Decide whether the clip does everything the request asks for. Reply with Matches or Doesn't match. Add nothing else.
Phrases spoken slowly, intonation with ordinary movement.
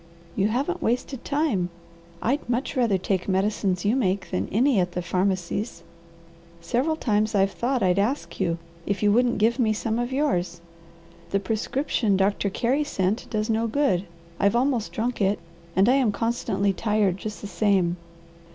Doesn't match